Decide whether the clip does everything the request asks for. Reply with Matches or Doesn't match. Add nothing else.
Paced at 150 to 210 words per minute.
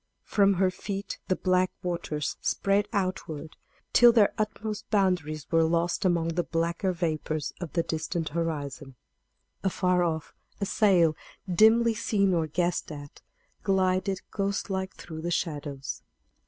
Doesn't match